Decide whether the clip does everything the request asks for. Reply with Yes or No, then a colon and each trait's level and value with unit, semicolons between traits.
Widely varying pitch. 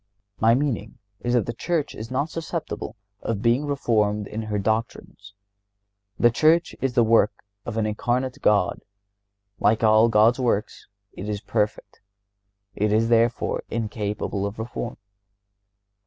No: narrow, 2.4 semitones